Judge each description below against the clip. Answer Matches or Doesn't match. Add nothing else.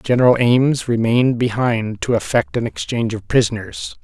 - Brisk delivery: Doesn't match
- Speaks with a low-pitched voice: Matches